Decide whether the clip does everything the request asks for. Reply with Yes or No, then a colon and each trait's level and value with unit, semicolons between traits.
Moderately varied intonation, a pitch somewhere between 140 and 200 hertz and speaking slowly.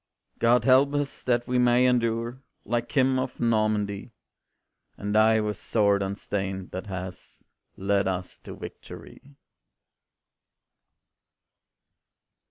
No: average, 3.6 semitones; low, 110 Hz; slow, 105 wpm